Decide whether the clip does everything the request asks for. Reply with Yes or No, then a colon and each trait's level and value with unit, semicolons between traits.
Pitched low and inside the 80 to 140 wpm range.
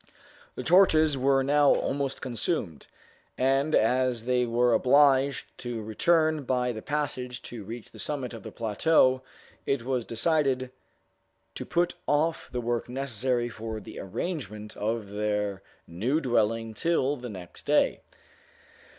Yes: low, 125 Hz; slow, 135 wpm